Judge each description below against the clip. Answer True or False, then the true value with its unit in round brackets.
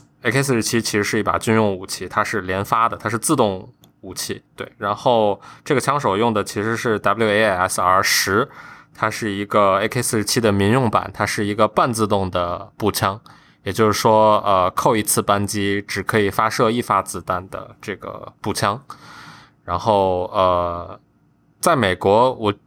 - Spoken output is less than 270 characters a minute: True (255 characters per minute)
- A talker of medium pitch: False (105 Hz)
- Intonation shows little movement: True (2.2 semitones)